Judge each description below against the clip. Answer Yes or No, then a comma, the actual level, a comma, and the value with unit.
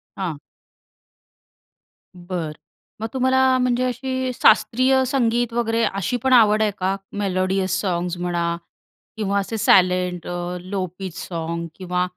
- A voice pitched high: Yes, high, 195 Hz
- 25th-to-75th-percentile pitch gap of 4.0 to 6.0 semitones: Yes, average, 5.1 semitones